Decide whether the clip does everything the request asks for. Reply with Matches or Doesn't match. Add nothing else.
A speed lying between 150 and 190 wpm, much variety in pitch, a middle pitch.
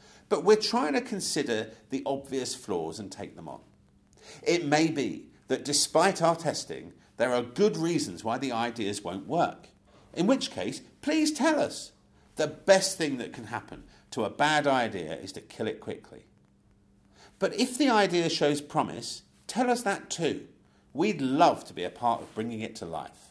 Matches